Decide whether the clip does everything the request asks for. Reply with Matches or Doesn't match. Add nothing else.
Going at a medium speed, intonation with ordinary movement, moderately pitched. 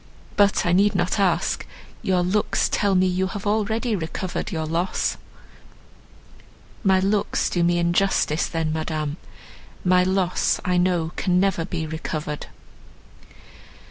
Doesn't match